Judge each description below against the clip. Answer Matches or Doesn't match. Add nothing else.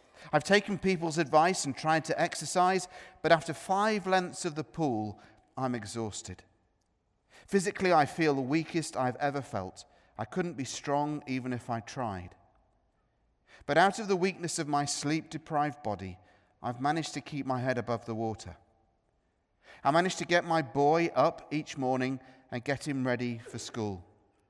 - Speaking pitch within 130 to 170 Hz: Matches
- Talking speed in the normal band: Matches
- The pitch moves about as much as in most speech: Doesn't match